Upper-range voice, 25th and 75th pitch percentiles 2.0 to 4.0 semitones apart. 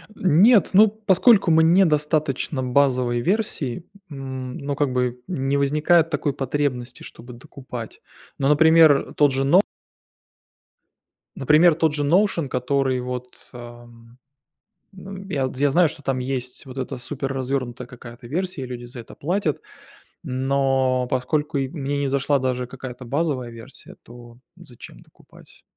No: low, 135 Hz; average, 3.4 semitones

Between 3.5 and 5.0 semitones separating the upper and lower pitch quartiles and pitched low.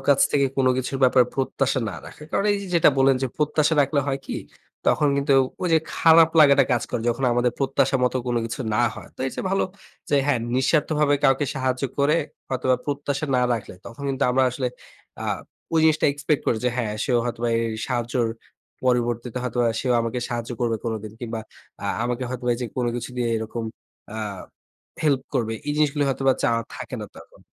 No: average, 2.8 semitones; low, 130 Hz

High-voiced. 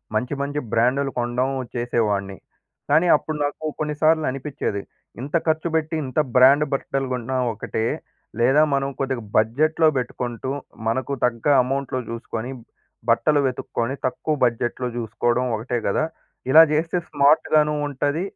No: low, 135 Hz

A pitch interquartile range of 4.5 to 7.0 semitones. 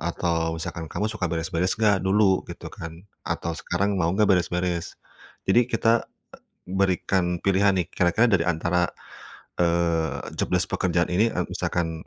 No: narrow, 2.5 semitones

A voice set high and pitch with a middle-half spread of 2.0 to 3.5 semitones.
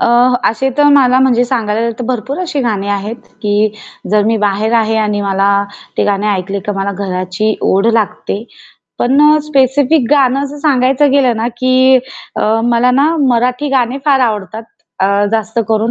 No: high, 235 Hz; average, 3.9 semitones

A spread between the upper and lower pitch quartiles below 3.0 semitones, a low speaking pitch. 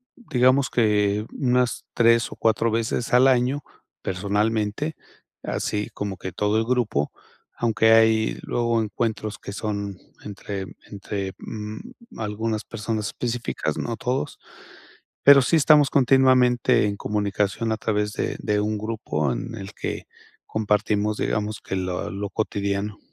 Yes: narrow, 2.6 semitones; low, 110 Hz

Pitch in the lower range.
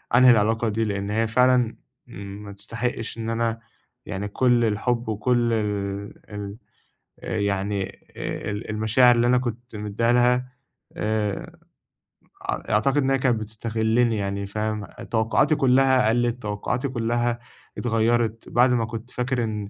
Yes: low, 115 Hz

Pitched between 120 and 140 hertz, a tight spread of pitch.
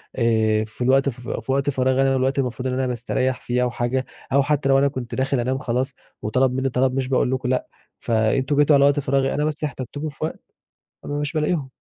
Yes: low, 130 Hz; narrow, 1.8 semitones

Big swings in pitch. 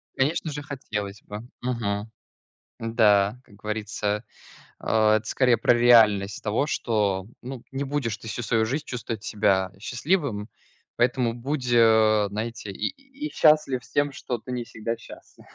No: average, 3.7 semitones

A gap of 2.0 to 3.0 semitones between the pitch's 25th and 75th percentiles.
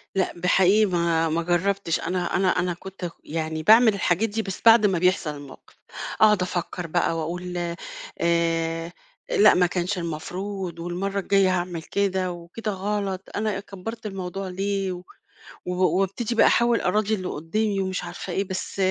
Yes: narrow, 2.5 semitones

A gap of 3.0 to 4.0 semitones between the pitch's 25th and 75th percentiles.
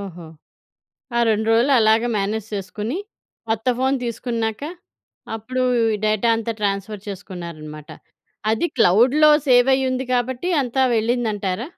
Yes: average, 3.5 semitones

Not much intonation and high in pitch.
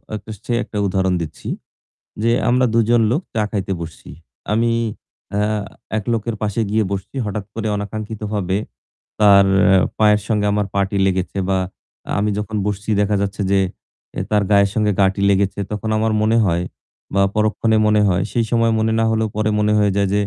No: narrow, 1.8 semitones; low, 105 Hz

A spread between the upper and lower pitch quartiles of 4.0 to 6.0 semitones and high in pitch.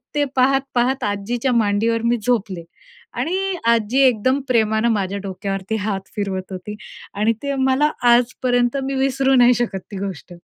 Yes: average, 4.3 semitones; high, 235 Hz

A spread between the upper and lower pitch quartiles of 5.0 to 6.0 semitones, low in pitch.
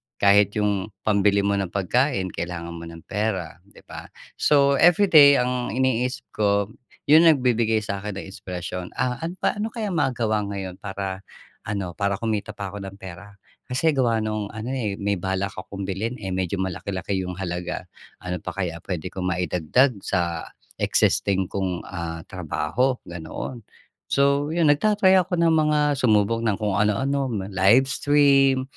Yes: wide, 5.6 semitones; low, 100 Hz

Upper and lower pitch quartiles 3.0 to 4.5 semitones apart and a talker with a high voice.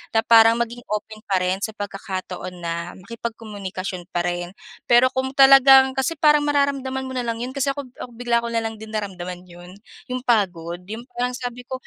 No: average, 5.1 semitones; high, 230 Hz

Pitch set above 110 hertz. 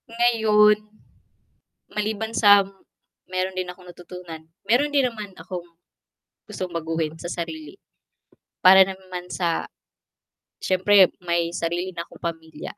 Yes: medium, 185 Hz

